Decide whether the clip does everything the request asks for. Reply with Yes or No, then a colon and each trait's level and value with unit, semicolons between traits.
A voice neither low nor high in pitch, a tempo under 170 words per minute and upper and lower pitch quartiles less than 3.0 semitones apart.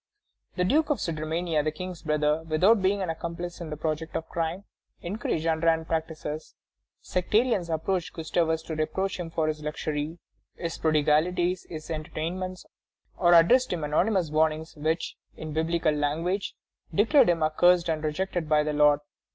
Yes: medium, 165 Hz; average, 150 wpm; narrow, 2.5 semitones